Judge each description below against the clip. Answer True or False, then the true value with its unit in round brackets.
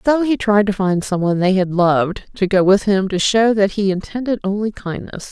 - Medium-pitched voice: False (200 Hz)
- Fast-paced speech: True (235 wpm)